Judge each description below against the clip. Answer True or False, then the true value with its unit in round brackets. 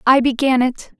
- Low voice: False (255 Hz)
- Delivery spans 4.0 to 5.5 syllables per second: True (4.7 syllables/s)